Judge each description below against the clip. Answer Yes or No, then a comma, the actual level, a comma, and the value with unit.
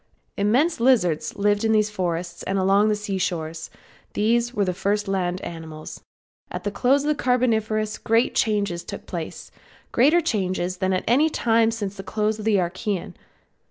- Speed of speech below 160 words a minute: No, average, 170 wpm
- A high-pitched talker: Yes, high, 210 Hz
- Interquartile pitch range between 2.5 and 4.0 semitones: Yes, average, 3.5 semitones